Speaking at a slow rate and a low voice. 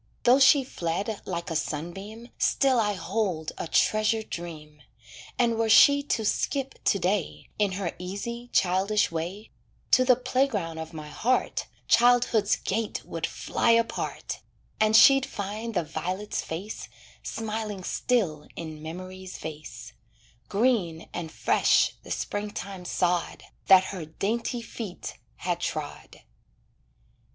No: slow, 125 wpm; high, 200 Hz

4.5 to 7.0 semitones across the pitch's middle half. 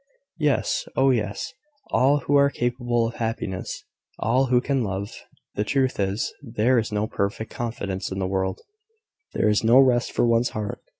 No: average, 3.8 semitones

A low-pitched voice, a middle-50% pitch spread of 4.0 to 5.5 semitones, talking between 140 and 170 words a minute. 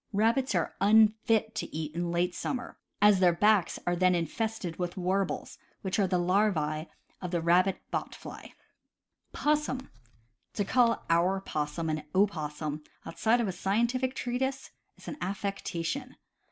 No: high, 190 Hz; average, 4.5 semitones; average, 150 wpm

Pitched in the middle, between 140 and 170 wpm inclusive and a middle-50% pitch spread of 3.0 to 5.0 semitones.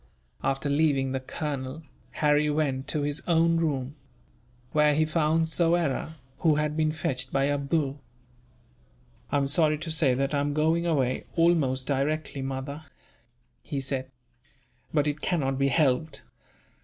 No: medium, 145 Hz; average, 145 wpm; narrow, 2.5 semitones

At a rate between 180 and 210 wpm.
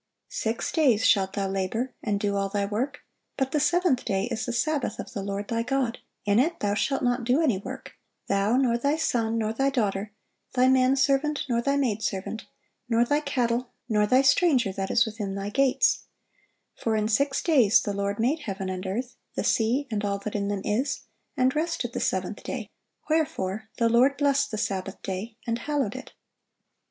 Yes: average, 195 wpm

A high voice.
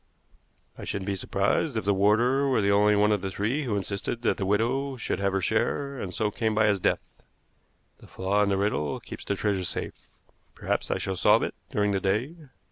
No: low, 105 Hz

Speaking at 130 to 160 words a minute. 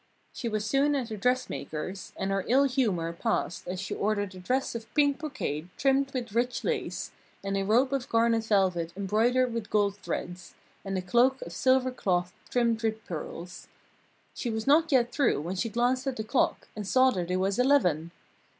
No: average, 190 wpm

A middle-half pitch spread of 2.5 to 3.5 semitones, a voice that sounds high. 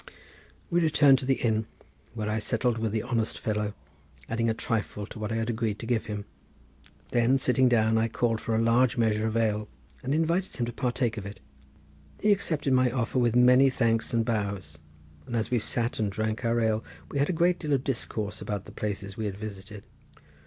No: average, 2.8 semitones; low, 115 Hz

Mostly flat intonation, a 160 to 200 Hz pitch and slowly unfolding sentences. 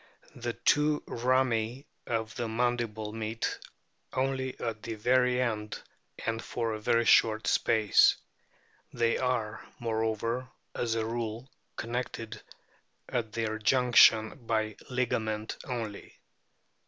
No: narrow, 2.0 semitones; low, 115 Hz; slow, 110 wpm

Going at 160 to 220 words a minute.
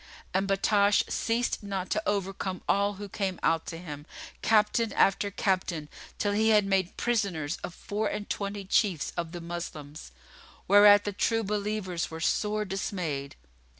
No: average, 150 wpm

